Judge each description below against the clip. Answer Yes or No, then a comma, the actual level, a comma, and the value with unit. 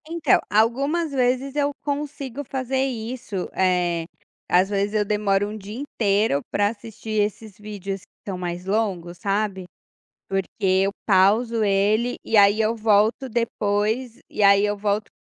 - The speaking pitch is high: Yes, high, 210 Hz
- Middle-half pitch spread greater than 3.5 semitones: No, average, 3.1 semitones